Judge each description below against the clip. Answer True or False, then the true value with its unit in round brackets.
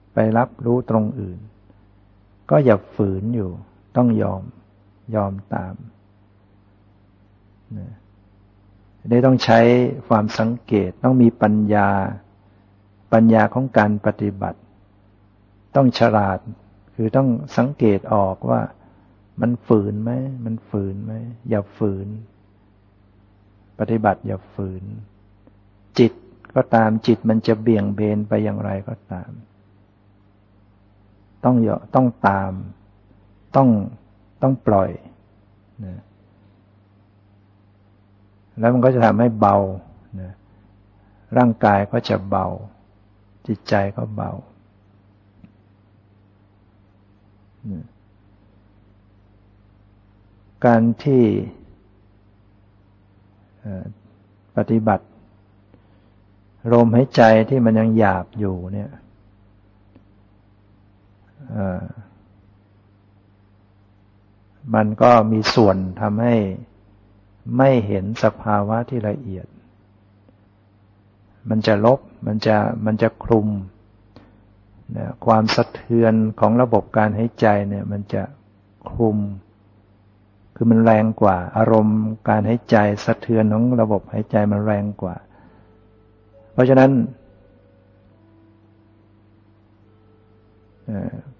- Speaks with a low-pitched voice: True (100 Hz)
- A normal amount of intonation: False (1.8 semitones)